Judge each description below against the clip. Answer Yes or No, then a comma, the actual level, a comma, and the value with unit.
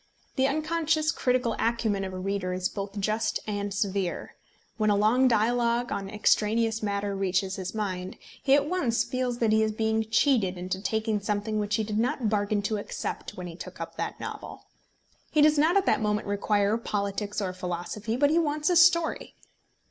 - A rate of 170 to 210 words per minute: Yes, average, 185 wpm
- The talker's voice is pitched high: Yes, high, 215 Hz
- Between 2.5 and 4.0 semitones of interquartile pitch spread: Yes, average, 3.5 semitones